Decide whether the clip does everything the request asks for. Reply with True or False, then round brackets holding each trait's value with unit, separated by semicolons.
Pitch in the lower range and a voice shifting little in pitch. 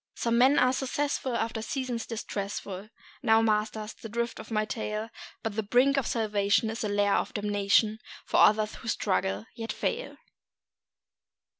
False (220 Hz; 2.2 semitones)